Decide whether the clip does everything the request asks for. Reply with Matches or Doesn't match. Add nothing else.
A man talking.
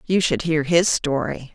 Doesn't match